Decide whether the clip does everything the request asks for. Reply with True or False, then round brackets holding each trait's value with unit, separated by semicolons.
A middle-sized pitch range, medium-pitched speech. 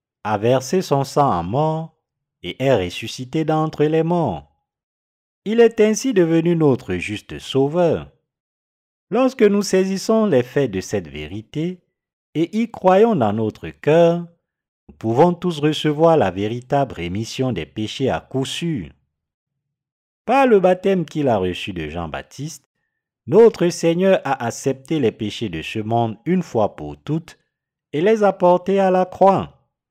False (8.5 semitones; 145 Hz)